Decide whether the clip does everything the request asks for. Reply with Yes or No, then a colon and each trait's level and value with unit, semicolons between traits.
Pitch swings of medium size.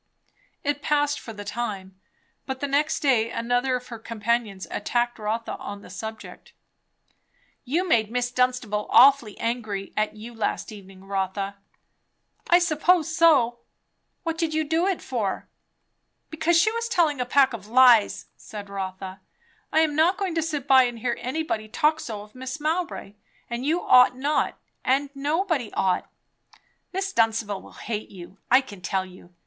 No: wide, 6.1 semitones